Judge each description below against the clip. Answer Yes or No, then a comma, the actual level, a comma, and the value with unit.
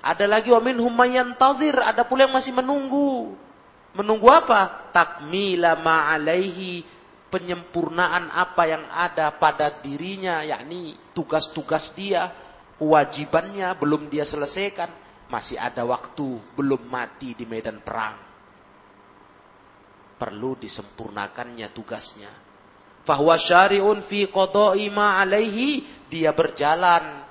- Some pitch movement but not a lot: No, wide, 6.9 semitones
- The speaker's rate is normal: Yes, average, 100 wpm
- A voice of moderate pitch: Yes, medium, 165 Hz